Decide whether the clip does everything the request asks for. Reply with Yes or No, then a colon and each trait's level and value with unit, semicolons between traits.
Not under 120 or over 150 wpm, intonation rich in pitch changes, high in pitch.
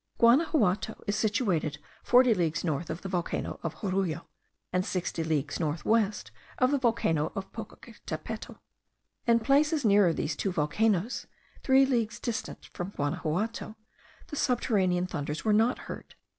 Yes: average, 140 wpm; wide, 5.7 semitones; high, 200 Hz